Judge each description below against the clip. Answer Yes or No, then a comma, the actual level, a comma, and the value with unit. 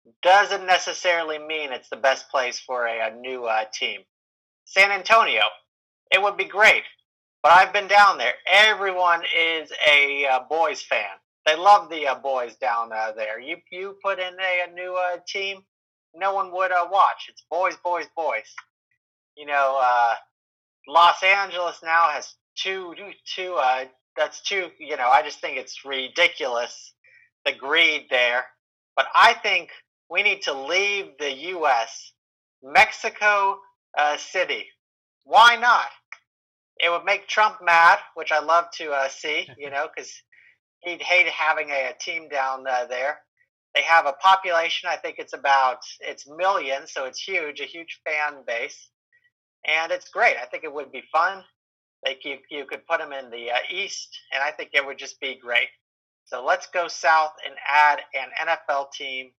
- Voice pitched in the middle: Yes, medium, 165 Hz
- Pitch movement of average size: No, wide, 6.2 semitones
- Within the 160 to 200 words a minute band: Yes, average, 170 wpm